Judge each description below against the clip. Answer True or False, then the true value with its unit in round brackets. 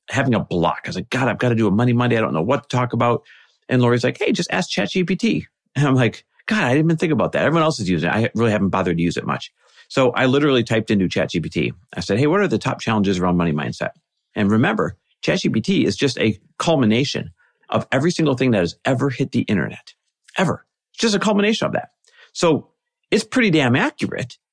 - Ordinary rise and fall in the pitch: False (6.2 semitones)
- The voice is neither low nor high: False (125 Hz)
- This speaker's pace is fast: True (240 wpm)